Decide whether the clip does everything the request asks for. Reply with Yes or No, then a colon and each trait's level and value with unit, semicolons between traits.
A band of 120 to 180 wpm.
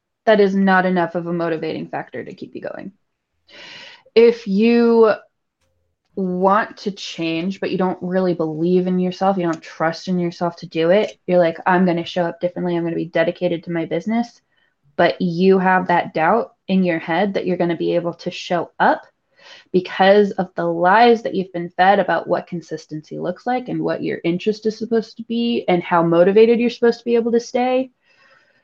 No: average, 195 wpm